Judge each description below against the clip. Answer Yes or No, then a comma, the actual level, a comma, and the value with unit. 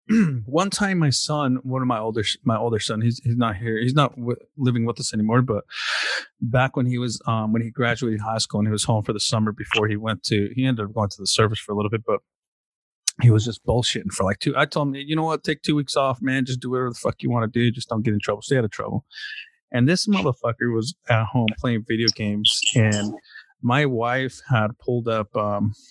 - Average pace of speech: No, fast, 250 wpm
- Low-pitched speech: Yes, low, 120 Hz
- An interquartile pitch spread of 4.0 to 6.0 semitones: No, average, 3.2 semitones